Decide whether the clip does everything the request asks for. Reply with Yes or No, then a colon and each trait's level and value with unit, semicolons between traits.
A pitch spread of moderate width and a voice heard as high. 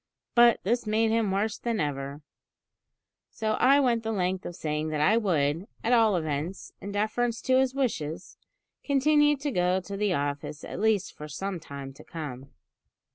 No: wide, 7.0 semitones; high, 200 Hz